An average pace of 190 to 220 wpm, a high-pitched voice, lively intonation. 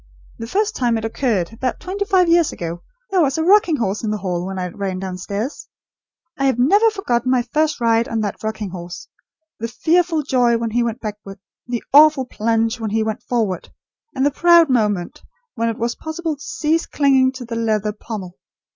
Yes: average, 200 wpm; high, 235 Hz; wide, 5.9 semitones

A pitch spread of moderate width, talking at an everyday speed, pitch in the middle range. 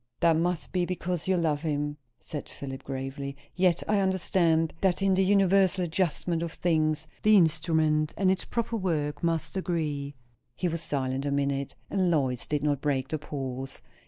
Yes: average, 3.9 semitones; average, 170 wpm; medium, 160 Hz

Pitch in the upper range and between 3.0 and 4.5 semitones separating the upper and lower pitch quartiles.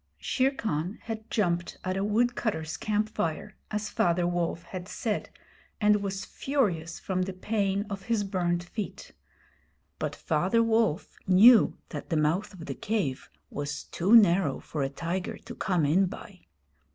Yes: high, 195 Hz; average, 3.8 semitones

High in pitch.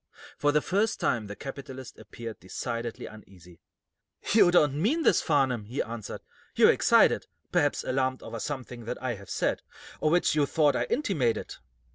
No: low, 130 Hz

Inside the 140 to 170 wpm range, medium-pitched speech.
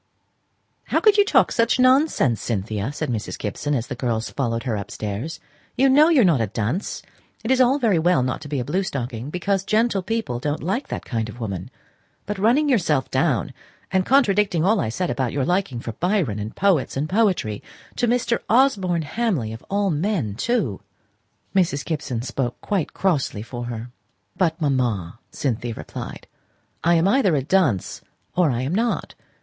No: average, 180 wpm; medium, 155 Hz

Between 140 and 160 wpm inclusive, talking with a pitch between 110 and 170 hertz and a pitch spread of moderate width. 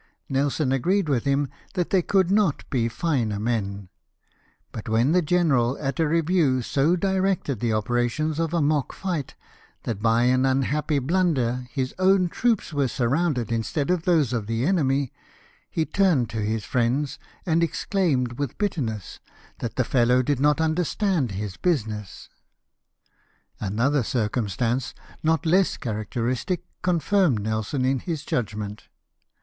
No: average, 145 wpm; low, 135 Hz; wide, 6.1 semitones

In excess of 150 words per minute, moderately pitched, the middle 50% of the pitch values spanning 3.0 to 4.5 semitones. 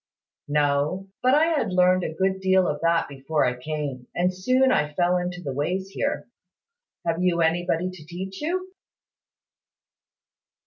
Yes: average, 160 wpm; medium, 180 Hz; average, 3.9 semitones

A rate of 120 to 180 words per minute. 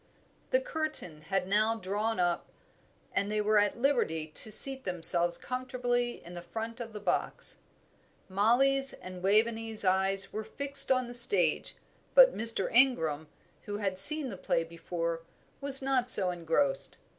Yes: average, 150 wpm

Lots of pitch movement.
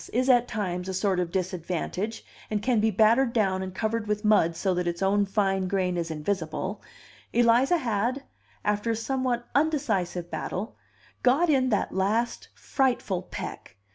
No: average, 4.3 semitones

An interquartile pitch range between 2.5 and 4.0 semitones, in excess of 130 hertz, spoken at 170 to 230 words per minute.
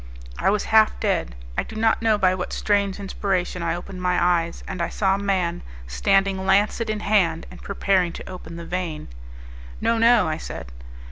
Yes: average, 2.9 semitones; high, 190 Hz; average, 190 wpm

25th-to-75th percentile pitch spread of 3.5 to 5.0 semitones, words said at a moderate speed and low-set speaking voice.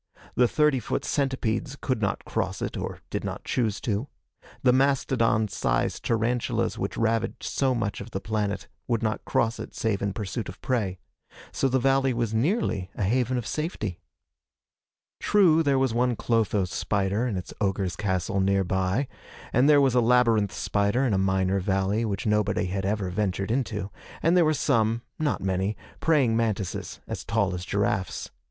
Yes: average, 4.5 semitones; average, 170 wpm; low, 110 Hz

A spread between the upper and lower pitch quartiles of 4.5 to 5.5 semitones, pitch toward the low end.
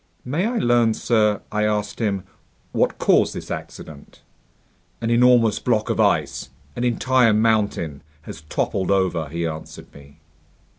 Yes: average, 5.1 semitones; low, 105 Hz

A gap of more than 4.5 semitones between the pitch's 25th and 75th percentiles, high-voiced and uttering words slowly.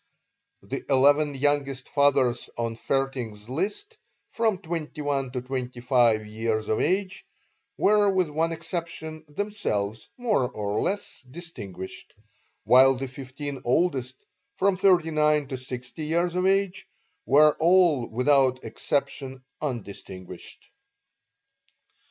No: average, 5.1 semitones; medium, 140 Hz; slow, 115 wpm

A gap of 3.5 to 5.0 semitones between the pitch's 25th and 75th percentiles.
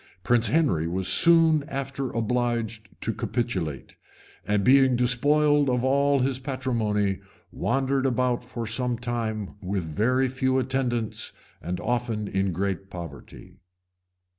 Yes: average, 4.2 semitones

